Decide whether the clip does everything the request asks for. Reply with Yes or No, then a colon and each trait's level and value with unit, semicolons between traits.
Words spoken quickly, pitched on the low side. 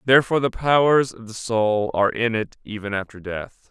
No: average, 195 wpm; low, 115 Hz